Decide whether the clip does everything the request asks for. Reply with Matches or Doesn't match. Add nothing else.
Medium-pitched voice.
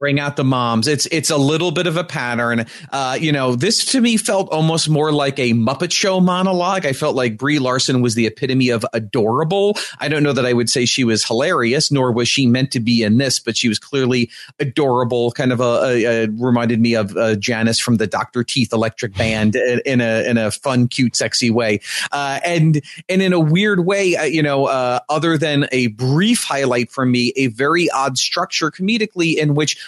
Doesn't match